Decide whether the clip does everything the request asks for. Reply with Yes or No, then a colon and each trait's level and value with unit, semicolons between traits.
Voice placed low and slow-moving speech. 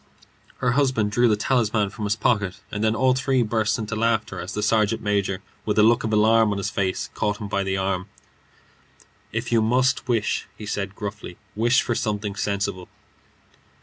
No: low, 105 Hz; average, 180 wpm